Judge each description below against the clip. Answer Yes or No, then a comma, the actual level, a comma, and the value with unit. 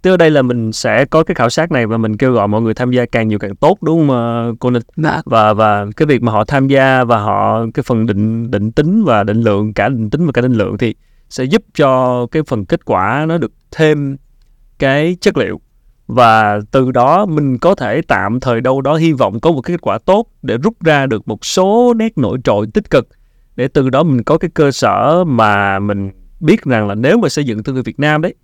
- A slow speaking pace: No, fast, 250 wpm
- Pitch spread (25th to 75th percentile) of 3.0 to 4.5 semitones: No, wide, 5.5 semitones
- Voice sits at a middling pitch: No, low, 125 Hz